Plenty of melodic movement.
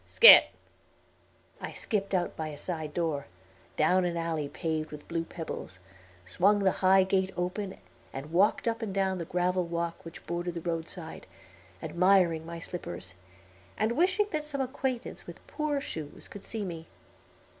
No: average, 3.4 semitones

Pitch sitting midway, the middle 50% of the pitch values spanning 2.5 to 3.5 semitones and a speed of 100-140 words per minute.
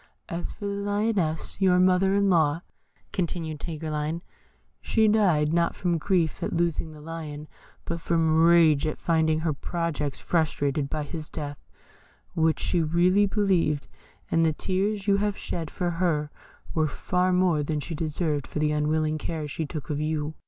No: medium, 165 Hz; average, 3.0 semitones; average, 165 wpm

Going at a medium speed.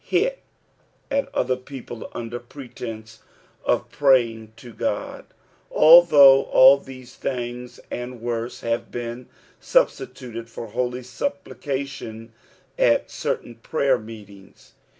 No: slow, 110 wpm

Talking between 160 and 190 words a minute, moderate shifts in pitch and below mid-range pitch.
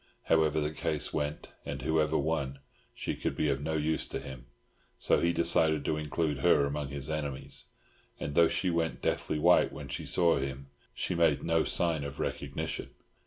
No: average, 180 wpm; narrow, 2.3 semitones; very low, 75 Hz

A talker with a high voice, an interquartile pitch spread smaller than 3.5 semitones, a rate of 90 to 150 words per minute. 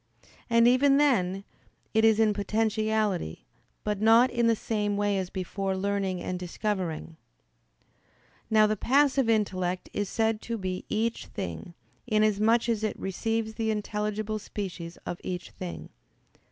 Yes: high, 210 Hz; average, 2.8 semitones; average, 140 wpm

